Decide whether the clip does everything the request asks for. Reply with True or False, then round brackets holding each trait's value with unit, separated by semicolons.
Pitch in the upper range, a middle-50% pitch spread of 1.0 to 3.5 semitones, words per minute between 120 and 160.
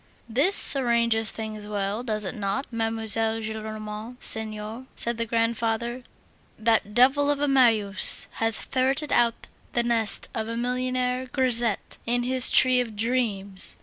True (230 Hz; 2.4 semitones; 140 wpm)